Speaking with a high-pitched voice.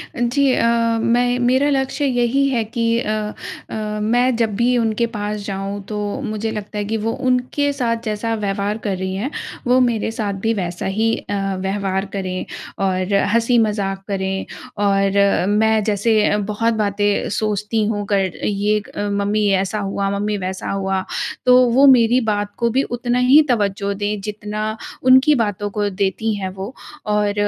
Yes: high, 210 Hz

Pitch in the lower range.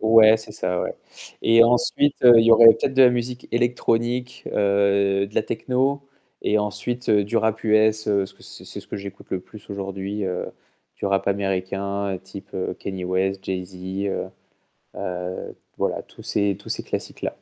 Yes: low, 100 Hz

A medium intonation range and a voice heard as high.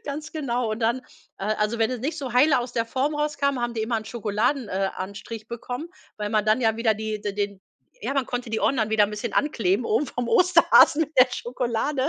Yes: average, 3.8 semitones; high, 235 Hz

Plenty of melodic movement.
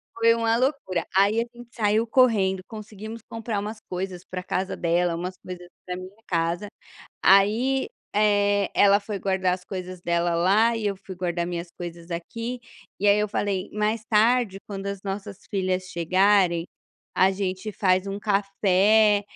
No: average, 2.7 semitones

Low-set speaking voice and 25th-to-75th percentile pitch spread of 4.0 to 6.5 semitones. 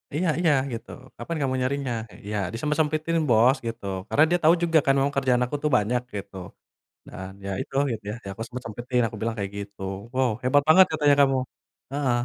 Yes: low, 130 Hz; average, 4.5 semitones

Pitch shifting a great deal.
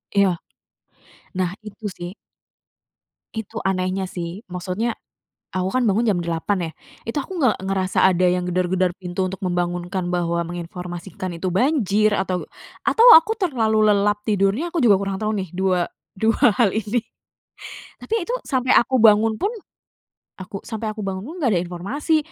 No: average, 3.6 semitones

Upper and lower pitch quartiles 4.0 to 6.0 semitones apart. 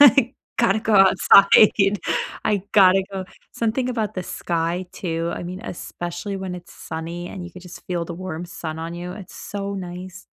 No: narrow, 2.4 semitones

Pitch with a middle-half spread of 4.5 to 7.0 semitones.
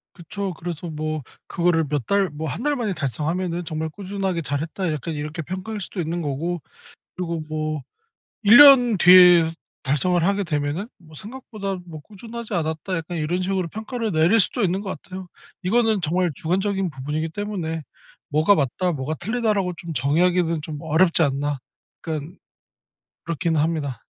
No: average, 3.8 semitones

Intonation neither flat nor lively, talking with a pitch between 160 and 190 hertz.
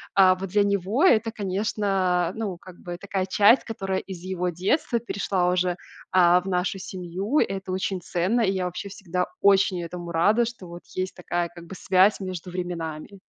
No: narrow, 2.1 semitones; medium, 185 Hz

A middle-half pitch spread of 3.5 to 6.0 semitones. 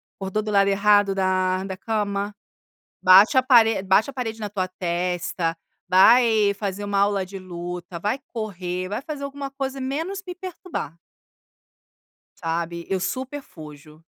Yes: average, 4.1 semitones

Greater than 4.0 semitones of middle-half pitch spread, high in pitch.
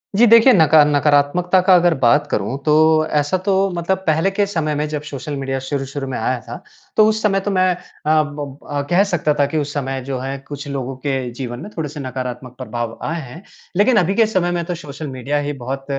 No: average, 4.6 semitones; medium, 145 Hz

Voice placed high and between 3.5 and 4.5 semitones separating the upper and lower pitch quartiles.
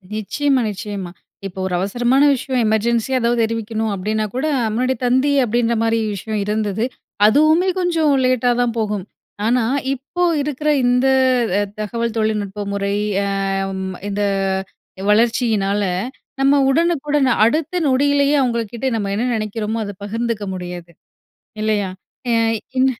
Yes: high, 230 Hz; average, 4.0 semitones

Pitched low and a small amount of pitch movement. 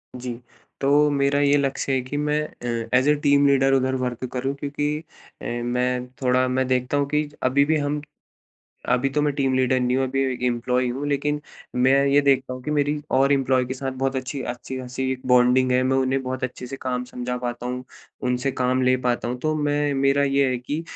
Yes: low, 130 Hz; narrow, 2.0 semitones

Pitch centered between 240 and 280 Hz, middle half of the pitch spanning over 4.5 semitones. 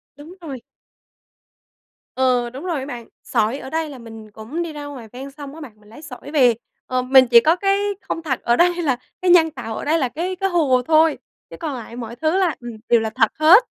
Yes: very high, 275 Hz; average, 5.1 semitones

